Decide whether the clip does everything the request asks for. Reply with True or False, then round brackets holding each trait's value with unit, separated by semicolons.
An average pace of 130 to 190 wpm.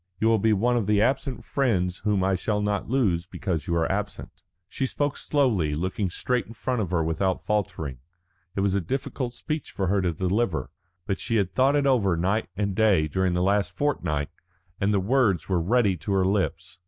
False (205 wpm)